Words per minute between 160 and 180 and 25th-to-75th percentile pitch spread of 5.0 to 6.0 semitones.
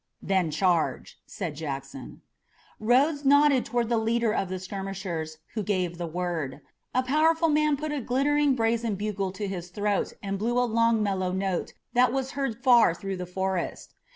Yes: average, 170 wpm; wide, 5.4 semitones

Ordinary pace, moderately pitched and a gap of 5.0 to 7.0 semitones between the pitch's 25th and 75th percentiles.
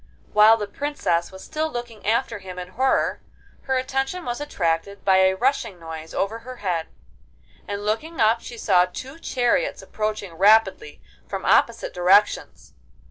No: average, 150 wpm; high, 215 Hz; wide, 5.5 semitones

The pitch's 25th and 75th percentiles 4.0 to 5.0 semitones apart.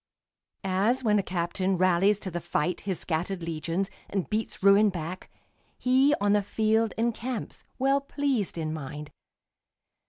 Yes: average, 4.3 semitones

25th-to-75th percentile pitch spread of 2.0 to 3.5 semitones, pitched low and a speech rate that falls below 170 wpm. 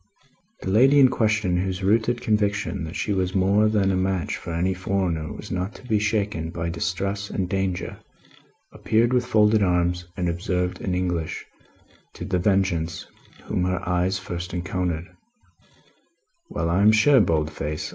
Yes: average, 2.9 semitones; very low, 95 Hz; average, 155 wpm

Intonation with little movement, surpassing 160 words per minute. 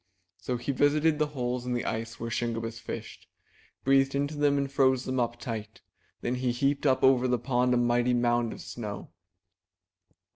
Yes: narrow, 2.3 semitones; average, 180 wpm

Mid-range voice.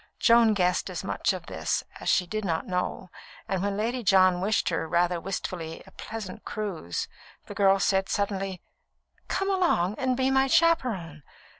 No: high, 195 Hz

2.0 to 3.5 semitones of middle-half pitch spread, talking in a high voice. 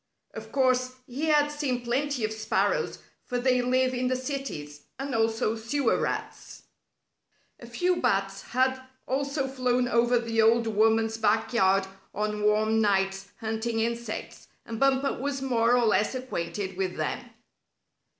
Yes: average, 2.9 semitones; high, 235 Hz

